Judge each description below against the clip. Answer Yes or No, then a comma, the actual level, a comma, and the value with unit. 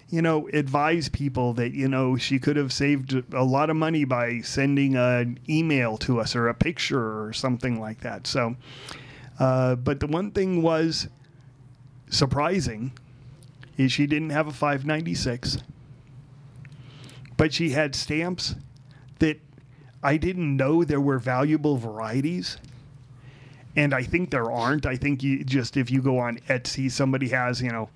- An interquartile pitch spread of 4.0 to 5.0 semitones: No, narrow, 2.4 semitones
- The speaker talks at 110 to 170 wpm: Yes, average, 155 wpm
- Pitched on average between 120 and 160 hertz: Yes, low, 135 Hz